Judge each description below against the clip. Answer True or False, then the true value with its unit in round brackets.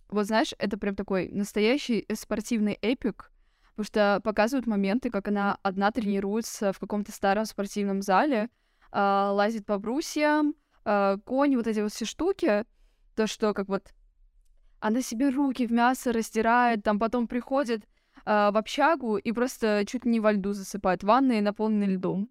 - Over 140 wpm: True (150 wpm)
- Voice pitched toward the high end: True (215 Hz)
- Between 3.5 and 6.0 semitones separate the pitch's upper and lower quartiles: False (2.9 semitones)